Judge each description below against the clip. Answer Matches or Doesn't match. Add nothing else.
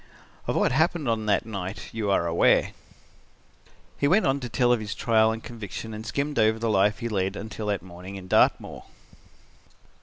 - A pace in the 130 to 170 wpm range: Doesn't match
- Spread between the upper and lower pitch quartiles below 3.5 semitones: Matches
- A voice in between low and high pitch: Doesn't match